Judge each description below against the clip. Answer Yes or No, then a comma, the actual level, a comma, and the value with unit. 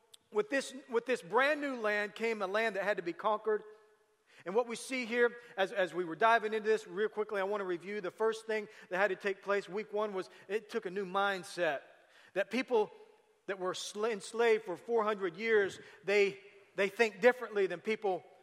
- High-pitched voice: Yes, high, 215 Hz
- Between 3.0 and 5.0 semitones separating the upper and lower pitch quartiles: No, narrow, 2.6 semitones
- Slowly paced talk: No, fast, 205 wpm